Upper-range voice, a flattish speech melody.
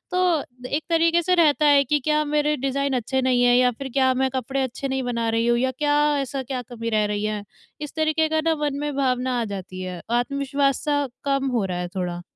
No: very high, 265 Hz; average, 3.6 semitones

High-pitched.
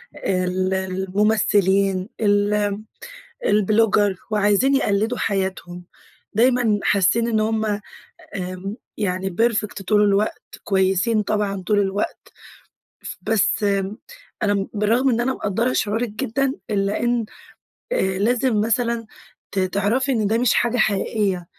Yes: high, 210 Hz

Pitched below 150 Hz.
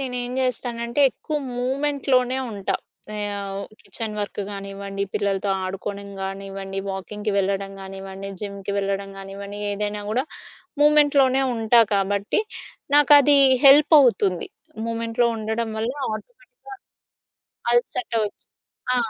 No: high, 210 Hz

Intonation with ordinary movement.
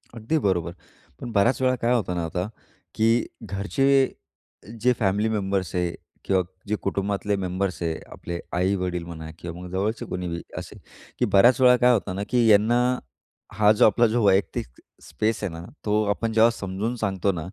Yes: average, 3.8 semitones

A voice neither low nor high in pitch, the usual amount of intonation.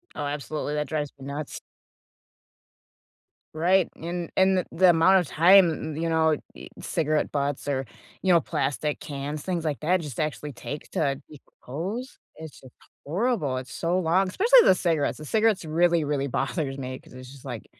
Yes: medium, 155 Hz; average, 3.6 semitones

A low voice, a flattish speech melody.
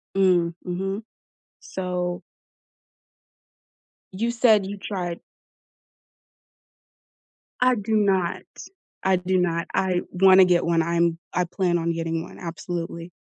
No: medium, 180 Hz; narrow, 2.2 semitones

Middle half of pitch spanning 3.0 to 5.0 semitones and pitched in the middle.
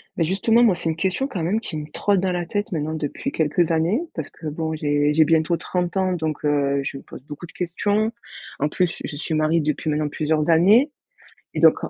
Yes: average, 3.4 semitones; medium, 165 Hz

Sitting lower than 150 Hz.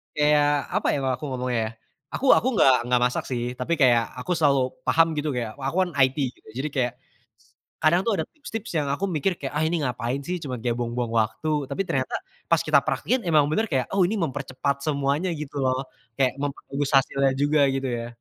Yes: medium, 140 Hz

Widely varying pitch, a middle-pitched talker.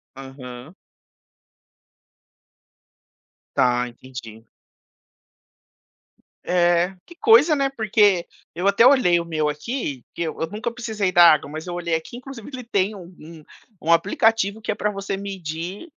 Yes: wide, 5.8 semitones; medium, 180 Hz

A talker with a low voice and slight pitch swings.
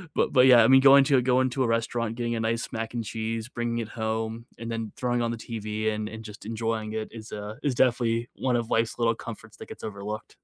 Yes: low, 115 Hz; narrow, 1.3 semitones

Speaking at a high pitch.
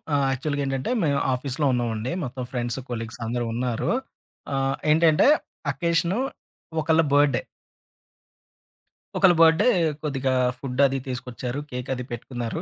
No: low, 135 Hz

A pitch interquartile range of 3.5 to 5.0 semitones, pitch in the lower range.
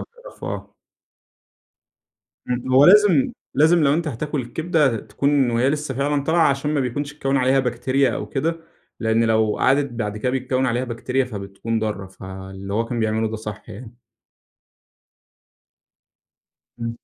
Yes: average, 4.3 semitones; low, 130 Hz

